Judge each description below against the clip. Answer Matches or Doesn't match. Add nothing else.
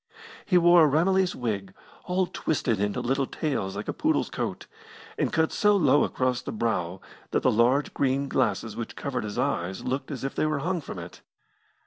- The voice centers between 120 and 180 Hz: Matches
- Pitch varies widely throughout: Matches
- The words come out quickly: Doesn't match